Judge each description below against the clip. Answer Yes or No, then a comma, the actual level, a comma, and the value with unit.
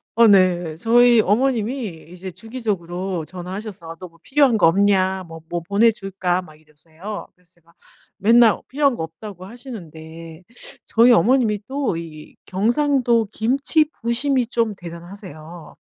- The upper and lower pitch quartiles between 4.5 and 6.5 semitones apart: Yes, wide, 5.5 semitones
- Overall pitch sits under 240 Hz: Yes, high, 195 Hz